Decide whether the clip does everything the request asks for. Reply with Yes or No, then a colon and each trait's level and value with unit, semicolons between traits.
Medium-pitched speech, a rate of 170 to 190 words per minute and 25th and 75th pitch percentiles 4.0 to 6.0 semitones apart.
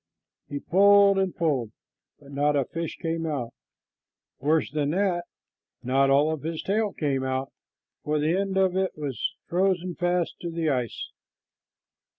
No: medium, 160 Hz; average, 155 wpm; average, 4.5 semitones